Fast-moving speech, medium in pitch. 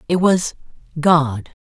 No: slow, 110 wpm; medium, 160 Hz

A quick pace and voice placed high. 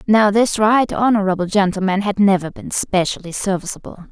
No: average, 145 wpm; high, 200 Hz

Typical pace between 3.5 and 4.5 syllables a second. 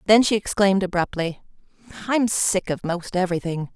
No: 5.5 syllables/s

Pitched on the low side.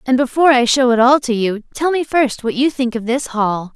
No: very high, 250 Hz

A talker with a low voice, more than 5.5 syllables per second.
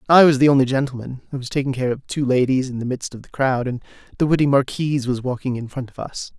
Yes: low, 130 Hz; 6.5 syllables/s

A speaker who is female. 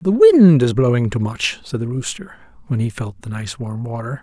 No: male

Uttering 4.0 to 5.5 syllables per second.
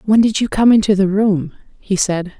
Yes: 5.0 syllables/s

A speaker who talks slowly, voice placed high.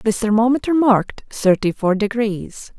Yes: slow, 130 wpm; high, 220 Hz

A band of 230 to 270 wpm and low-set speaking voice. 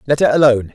Yes: fast, 240 wpm; low, 130 Hz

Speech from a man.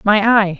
No: female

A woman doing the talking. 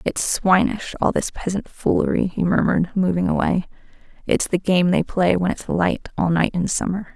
Yes: female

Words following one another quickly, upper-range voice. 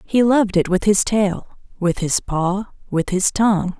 No: average, 190 wpm; high, 195 Hz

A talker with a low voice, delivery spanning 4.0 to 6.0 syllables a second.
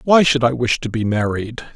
Yes: low, 125 Hz; 5.2 syllables/s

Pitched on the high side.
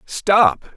No: medium, 180 Hz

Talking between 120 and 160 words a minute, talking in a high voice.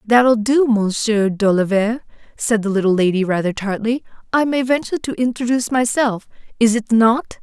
Yes: average, 155 wpm; high, 225 Hz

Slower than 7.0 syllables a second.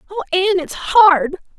No: 7.1 syllables/s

